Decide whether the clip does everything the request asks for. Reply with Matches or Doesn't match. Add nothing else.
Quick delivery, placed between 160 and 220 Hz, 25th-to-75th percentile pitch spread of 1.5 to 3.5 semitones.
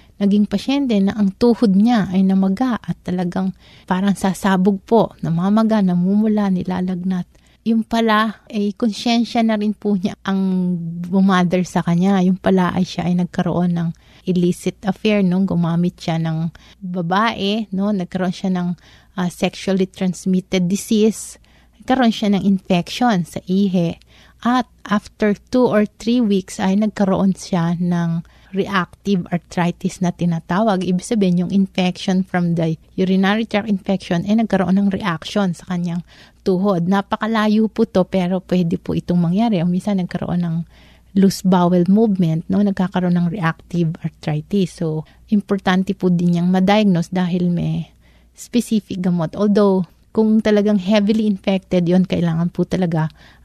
Doesn't match